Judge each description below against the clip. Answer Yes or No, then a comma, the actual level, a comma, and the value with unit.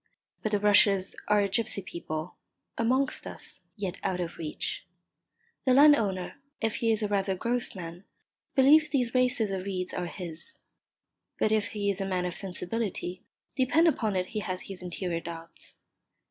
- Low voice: No, high, 200 Hz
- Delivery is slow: No, average, 165 wpm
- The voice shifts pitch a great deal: No, average, 4.1 semitones